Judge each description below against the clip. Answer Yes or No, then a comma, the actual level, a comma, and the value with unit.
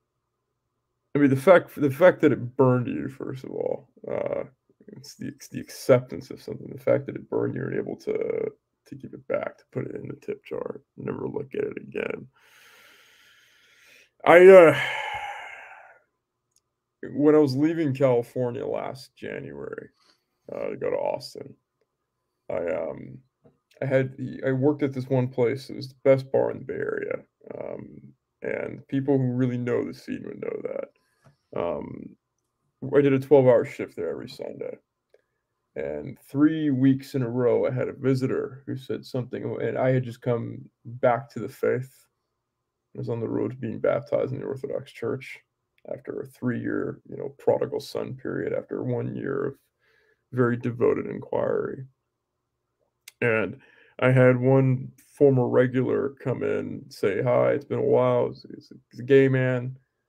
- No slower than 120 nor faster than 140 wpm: No, average, 170 wpm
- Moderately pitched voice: Yes, medium, 145 Hz